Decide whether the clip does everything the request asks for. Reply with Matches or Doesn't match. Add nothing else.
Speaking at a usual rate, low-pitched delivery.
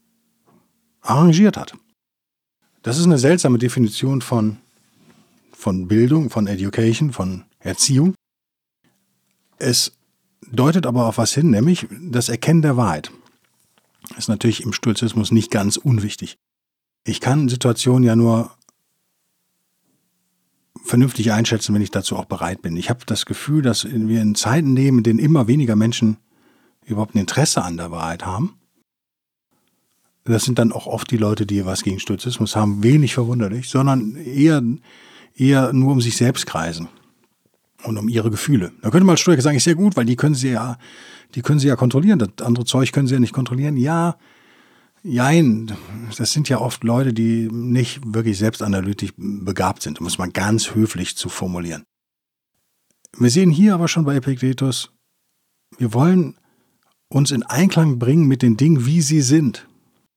Matches